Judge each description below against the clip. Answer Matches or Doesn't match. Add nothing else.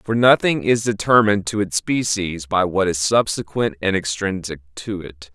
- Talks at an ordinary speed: Matches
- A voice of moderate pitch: Doesn't match